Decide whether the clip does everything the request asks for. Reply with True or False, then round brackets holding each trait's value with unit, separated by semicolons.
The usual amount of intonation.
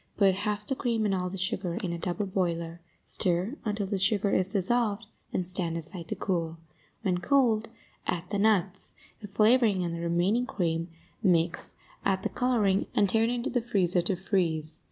True (3.5 semitones)